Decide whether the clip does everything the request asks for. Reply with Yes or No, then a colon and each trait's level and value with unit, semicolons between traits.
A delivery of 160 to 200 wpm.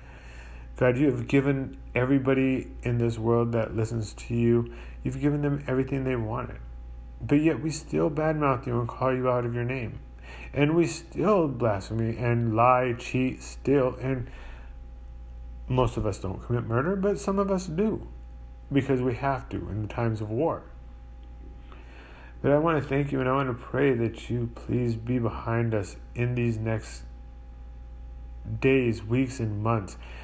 Yes: average, 165 wpm